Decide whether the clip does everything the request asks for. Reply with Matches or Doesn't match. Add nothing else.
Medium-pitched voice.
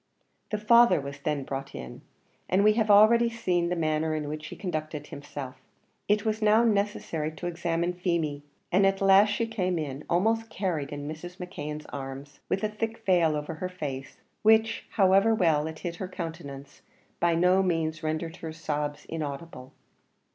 Matches